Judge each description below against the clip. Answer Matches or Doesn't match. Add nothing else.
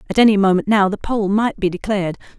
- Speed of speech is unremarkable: Doesn't match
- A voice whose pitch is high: Matches